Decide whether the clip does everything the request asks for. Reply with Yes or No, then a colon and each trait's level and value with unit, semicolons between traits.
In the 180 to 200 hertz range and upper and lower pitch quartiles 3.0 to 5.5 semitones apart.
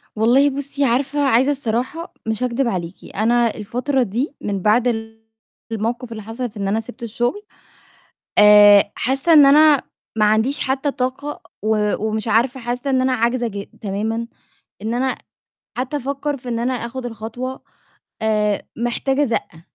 No: high, 240 Hz; average, 3.3 semitones